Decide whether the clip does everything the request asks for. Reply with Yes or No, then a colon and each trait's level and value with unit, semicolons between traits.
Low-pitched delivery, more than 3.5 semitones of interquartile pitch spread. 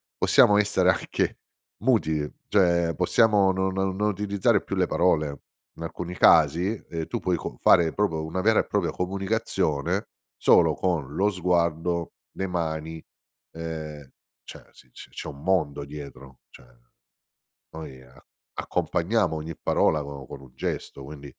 Yes: very low, 85 Hz; average, 4.0 semitones